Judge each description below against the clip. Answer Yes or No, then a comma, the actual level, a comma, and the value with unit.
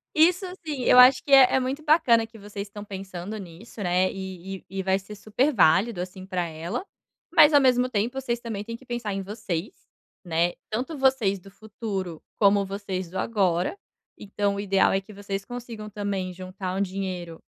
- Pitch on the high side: Yes, high, 200 Hz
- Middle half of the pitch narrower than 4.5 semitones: Yes, average, 4.0 semitones